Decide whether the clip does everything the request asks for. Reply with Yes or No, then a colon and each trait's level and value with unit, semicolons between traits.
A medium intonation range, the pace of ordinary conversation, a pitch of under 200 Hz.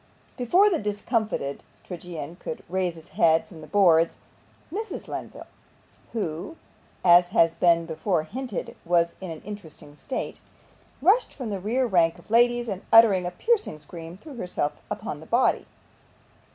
No: wide, 5.7 semitones; average, 150 wpm; medium, 185 Hz